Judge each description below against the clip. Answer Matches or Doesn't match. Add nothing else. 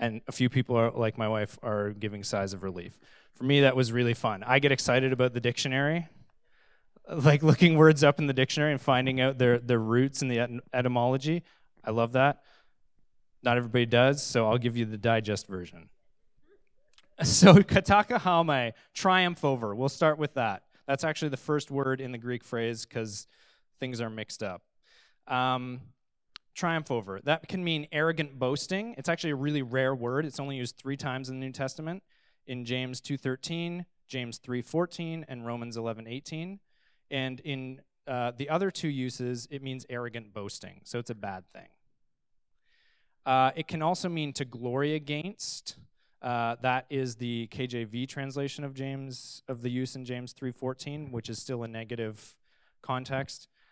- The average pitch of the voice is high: Doesn't match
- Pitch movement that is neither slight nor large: Matches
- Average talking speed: Matches